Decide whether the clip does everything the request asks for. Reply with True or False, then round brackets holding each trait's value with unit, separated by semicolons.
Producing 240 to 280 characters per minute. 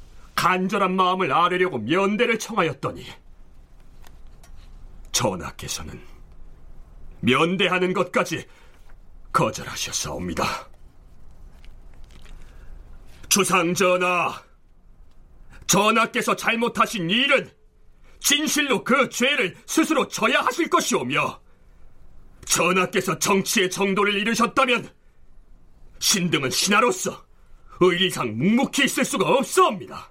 False (210 characters per minute)